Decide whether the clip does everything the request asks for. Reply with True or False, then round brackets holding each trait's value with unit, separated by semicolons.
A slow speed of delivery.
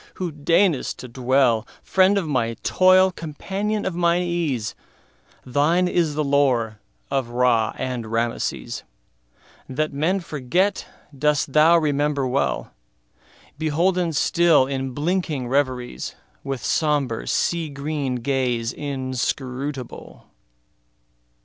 True (90 wpm)